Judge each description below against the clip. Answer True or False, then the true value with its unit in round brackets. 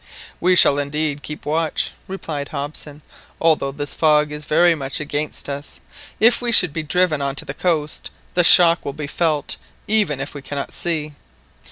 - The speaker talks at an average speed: True (175 wpm)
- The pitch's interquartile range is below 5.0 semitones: True (2.6 semitones)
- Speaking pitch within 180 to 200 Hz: False (150 Hz)